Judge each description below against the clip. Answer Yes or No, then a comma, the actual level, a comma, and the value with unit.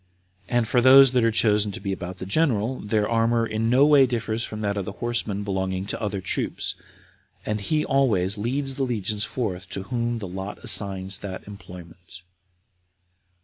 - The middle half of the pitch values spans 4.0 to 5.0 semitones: No, average, 3.6 semitones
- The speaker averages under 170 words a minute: No, average, 175 wpm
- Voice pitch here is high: No, low, 105 Hz